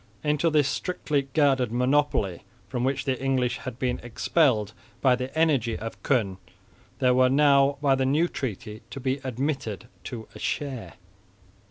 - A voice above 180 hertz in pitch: No, low, 130 Hz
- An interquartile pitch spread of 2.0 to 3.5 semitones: Yes, average, 2.7 semitones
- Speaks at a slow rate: No, average, 155 wpm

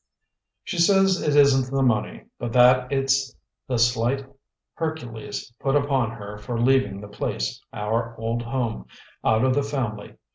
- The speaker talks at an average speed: Yes, average, 150 wpm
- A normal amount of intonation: Yes, average, 3.1 semitones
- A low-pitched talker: Yes, low, 125 Hz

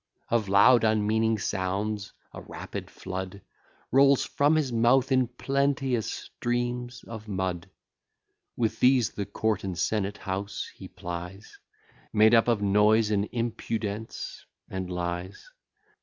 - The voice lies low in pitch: Yes, low, 110 Hz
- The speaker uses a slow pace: Yes, slow, 125 wpm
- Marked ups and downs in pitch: No, average, 3.7 semitones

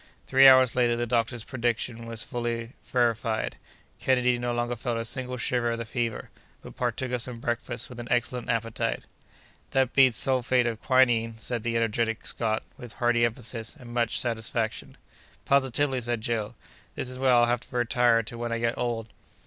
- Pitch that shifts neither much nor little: No, narrow, 1.4 semitones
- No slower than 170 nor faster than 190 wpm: Yes, average, 180 wpm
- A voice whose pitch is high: No, low, 120 Hz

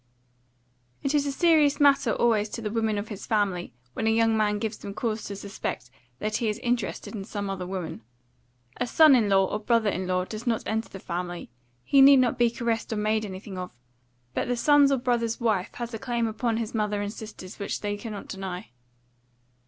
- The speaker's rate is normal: No, fast, 210 wpm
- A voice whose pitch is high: Yes, high, 220 Hz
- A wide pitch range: No, average, 2.9 semitones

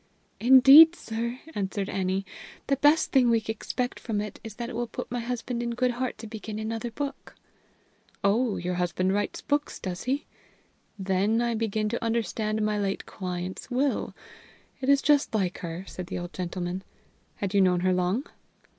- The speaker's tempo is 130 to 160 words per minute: No, average, 175 wpm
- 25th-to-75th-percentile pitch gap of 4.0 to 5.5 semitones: Yes, average, 4.4 semitones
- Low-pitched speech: No, high, 220 Hz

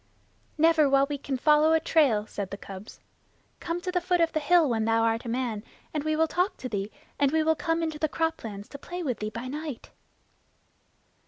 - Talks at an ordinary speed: No, fast, 220 wpm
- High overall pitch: Yes, very high, 295 Hz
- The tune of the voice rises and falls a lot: Yes, wide, 6.0 semitones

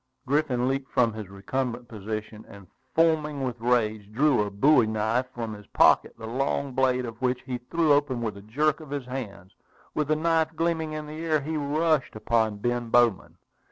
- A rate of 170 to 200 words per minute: Yes, average, 190 wpm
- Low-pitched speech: Yes, low, 125 Hz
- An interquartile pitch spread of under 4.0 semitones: No, average, 5.3 semitones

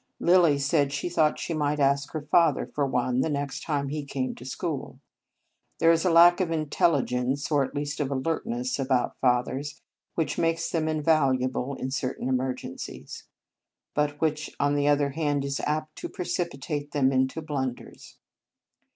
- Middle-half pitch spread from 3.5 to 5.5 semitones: No, average, 2.8 semitones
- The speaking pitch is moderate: Yes, medium, 145 Hz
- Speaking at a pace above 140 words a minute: Yes, average, 170 wpm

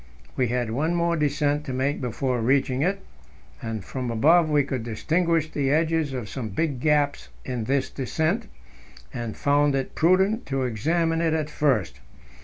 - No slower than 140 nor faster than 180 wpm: Yes, average, 160 wpm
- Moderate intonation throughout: Yes, average, 4.2 semitones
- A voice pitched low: No, medium, 145 Hz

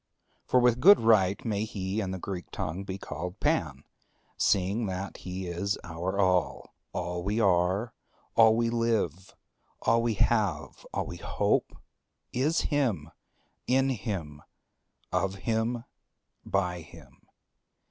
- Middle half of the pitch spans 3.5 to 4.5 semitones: Yes, average, 4.2 semitones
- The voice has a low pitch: Yes, low, 100 Hz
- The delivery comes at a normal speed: No, slow, 130 wpm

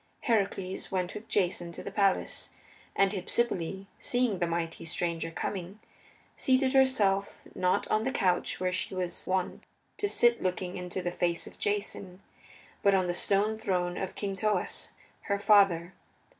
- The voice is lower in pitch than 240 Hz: Yes, high, 190 Hz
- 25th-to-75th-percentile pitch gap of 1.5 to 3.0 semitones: Yes, narrow, 2.5 semitones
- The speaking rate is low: No, average, 155 wpm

